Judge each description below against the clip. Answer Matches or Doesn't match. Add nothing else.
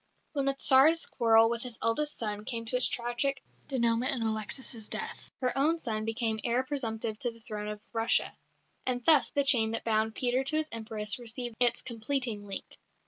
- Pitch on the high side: Matches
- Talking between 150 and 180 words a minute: Doesn't match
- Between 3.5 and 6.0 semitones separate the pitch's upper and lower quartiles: Doesn't match